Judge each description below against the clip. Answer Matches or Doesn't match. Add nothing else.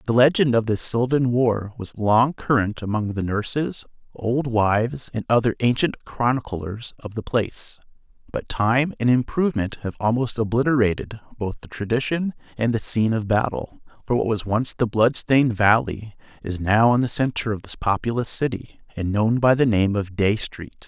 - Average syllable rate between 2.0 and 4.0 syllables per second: Doesn't match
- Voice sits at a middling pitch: Doesn't match